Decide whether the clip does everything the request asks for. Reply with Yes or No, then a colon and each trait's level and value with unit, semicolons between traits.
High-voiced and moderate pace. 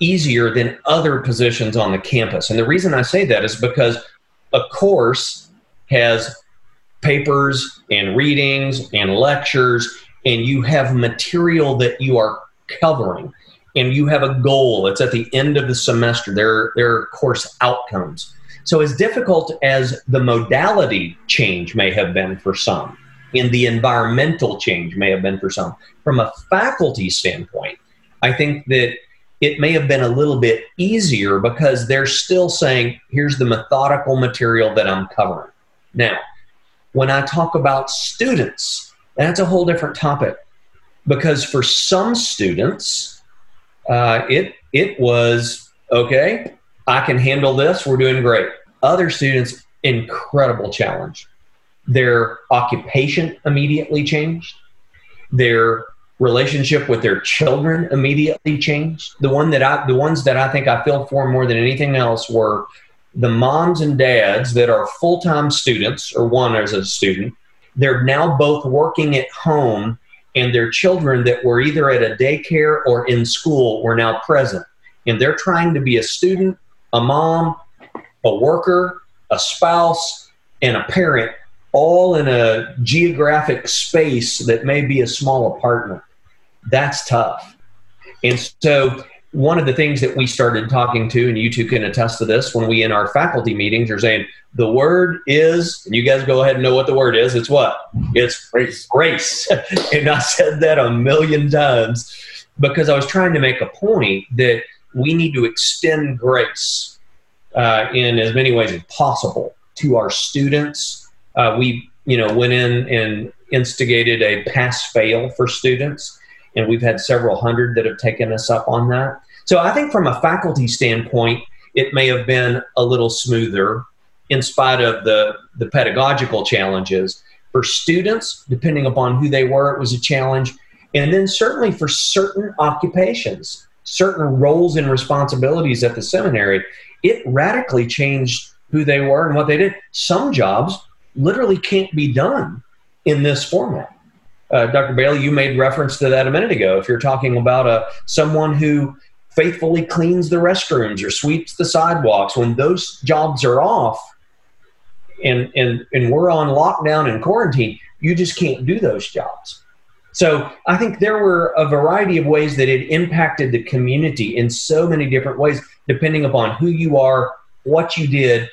No: low, 135 Hz; average, 160 wpm